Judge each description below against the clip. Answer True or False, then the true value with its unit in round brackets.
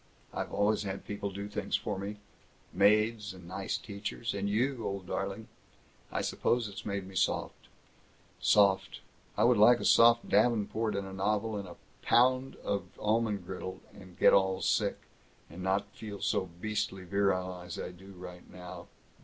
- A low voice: True (100 Hz)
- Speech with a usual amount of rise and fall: False (2.2 semitones)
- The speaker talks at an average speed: True (170 wpm)